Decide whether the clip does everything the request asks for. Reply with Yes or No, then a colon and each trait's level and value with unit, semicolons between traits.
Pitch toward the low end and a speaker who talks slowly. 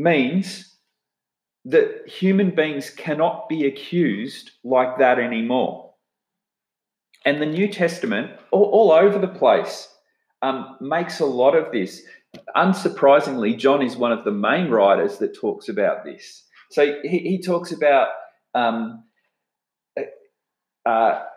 No: high, 190 Hz; slow, 125 wpm